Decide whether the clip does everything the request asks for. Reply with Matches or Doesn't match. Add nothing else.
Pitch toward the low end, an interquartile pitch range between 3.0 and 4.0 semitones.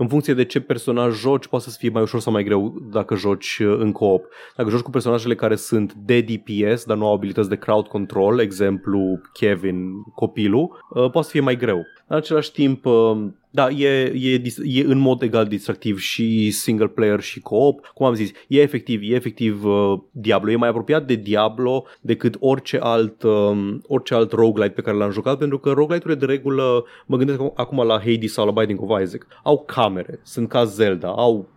Matches